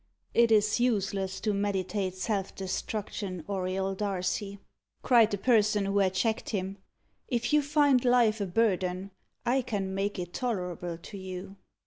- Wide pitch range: No, average, 3.0 semitones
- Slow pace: No, average, 145 wpm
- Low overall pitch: No, high, 200 Hz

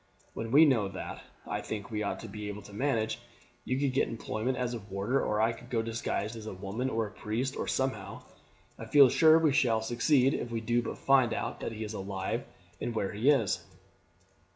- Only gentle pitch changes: No, average, 3.4 semitones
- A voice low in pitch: Yes, low, 115 Hz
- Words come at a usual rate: No, fast, 225 wpm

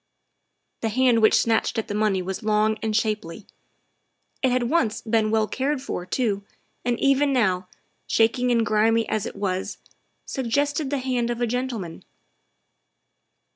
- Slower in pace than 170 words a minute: Yes, average, 160 wpm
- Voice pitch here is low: No, high, 225 Hz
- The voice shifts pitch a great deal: No, average, 3.1 semitones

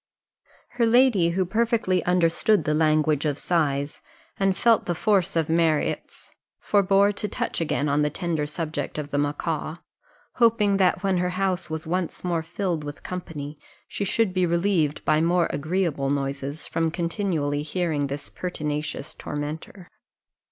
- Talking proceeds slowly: No, average, 150 wpm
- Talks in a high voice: No, medium, 170 Hz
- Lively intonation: No, average, 3.9 semitones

